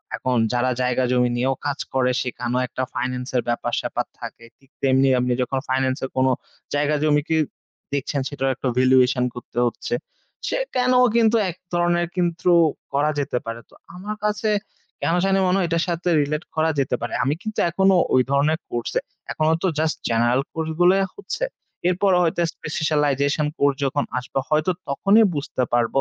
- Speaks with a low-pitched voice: No, medium, 145 Hz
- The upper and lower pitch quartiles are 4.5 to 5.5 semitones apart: Yes, average, 5.1 semitones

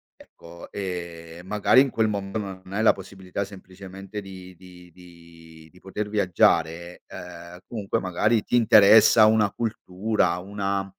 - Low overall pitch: Yes, very low, 95 Hz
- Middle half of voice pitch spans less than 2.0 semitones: No, average, 2.7 semitones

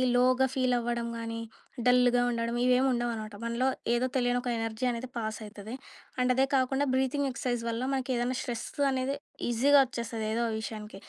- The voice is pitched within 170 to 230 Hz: No, high, 245 Hz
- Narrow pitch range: Yes, narrow, 1.8 semitones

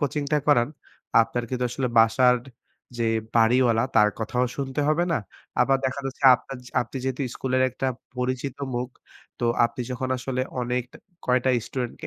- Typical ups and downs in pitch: No, narrow, 1.6 semitones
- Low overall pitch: Yes, low, 125 Hz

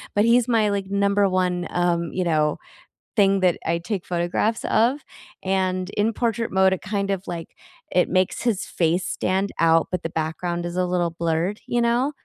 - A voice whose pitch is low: No, medium, 185 Hz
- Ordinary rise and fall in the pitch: Yes, average, 3.0 semitones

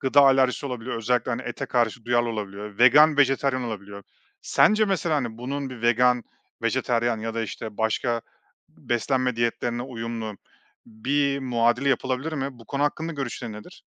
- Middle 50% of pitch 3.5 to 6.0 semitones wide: No, average, 2.9 semitones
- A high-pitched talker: No, low, 125 Hz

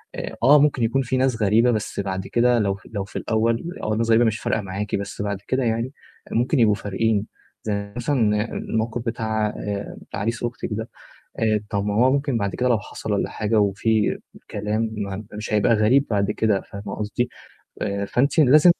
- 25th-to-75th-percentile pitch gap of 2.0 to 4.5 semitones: Yes, average, 2.7 semitones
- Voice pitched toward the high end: No, low, 110 Hz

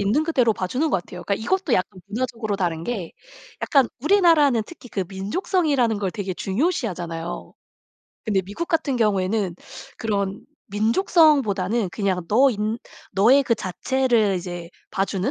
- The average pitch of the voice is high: Yes, high, 215 Hz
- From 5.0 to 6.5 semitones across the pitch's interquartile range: Yes, wide, 5.6 semitones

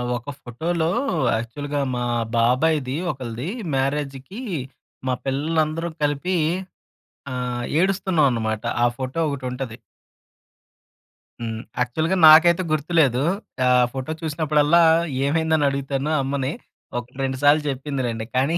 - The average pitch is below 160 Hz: Yes, medium, 140 Hz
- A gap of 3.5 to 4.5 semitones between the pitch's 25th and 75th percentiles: Yes, average, 3.8 semitones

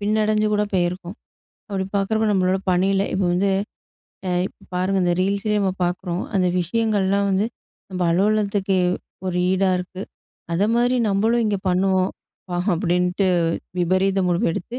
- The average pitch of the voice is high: Yes, high, 195 Hz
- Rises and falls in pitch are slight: Yes, narrow, 2.1 semitones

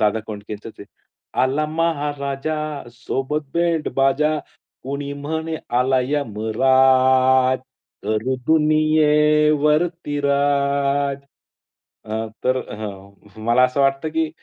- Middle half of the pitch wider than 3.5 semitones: No, average, 3.0 semitones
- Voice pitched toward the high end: No, medium, 140 Hz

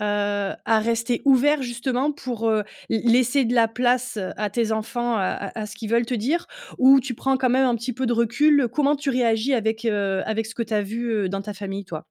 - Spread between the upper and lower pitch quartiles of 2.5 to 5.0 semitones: Yes, average, 2.9 semitones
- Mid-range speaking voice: No, high, 230 Hz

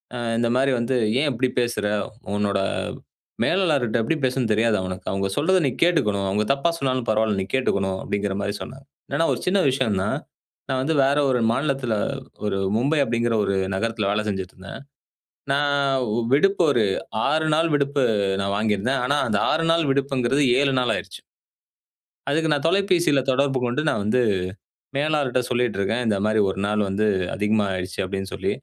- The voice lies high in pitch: No, low, 125 Hz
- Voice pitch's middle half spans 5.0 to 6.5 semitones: Yes, average, 5.3 semitones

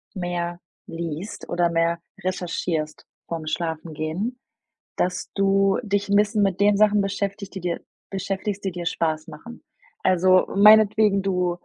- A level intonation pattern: No, average, 3.0 semitones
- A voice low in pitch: No, medium, 185 Hz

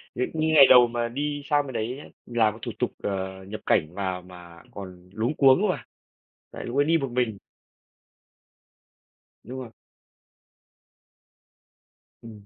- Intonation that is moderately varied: No, wide, 5.7 semitones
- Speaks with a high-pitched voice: No, low, 115 Hz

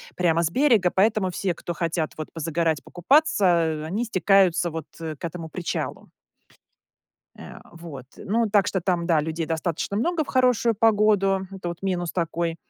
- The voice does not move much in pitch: No, average, 3.7 semitones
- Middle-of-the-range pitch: Yes, medium, 175 Hz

